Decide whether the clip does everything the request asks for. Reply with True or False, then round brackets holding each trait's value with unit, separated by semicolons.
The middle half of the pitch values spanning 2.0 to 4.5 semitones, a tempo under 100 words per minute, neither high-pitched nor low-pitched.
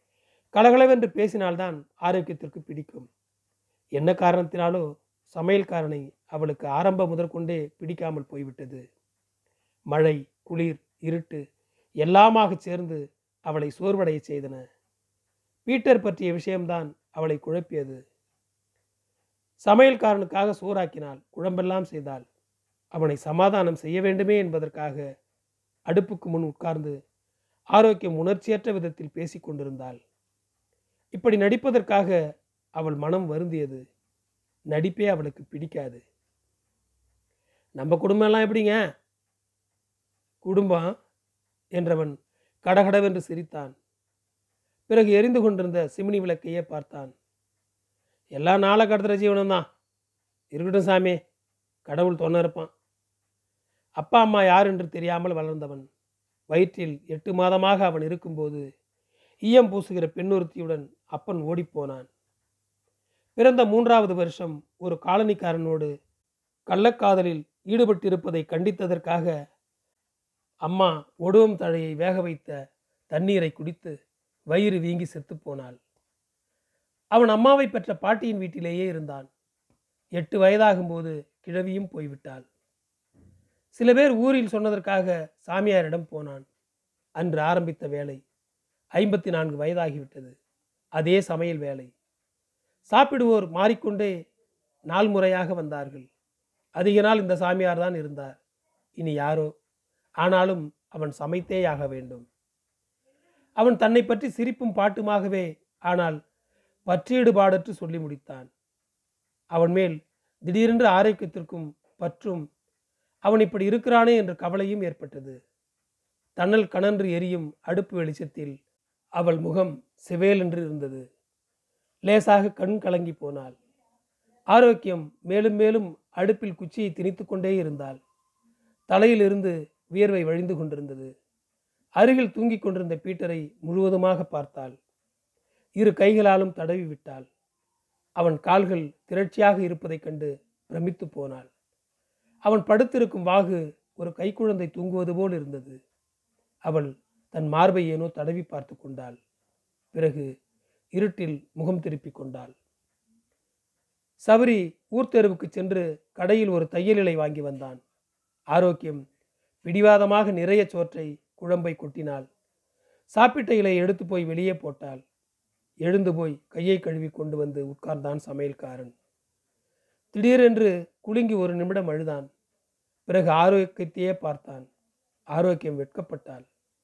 False (5.3 semitones; 90 wpm; 170 Hz)